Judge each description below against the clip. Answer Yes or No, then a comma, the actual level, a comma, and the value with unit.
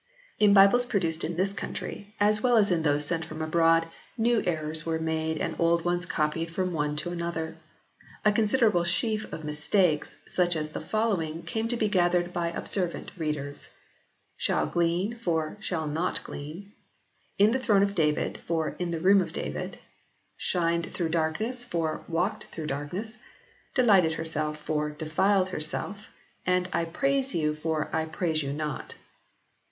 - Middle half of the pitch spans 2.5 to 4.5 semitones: Yes, average, 4.1 semitones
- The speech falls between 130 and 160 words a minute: No, average, 185 wpm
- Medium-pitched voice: Yes, medium, 170 Hz